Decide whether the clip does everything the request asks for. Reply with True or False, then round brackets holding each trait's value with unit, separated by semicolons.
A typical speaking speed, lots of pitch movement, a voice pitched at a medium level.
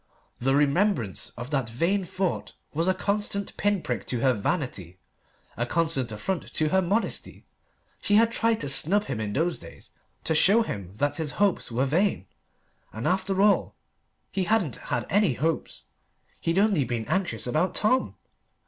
True (165 wpm; 7.8 semitones; 165 Hz)